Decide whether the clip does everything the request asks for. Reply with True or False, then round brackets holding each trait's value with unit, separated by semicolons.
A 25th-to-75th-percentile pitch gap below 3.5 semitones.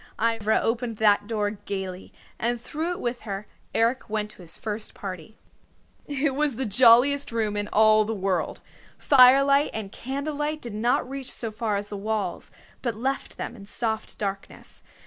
False (3.8 semitones)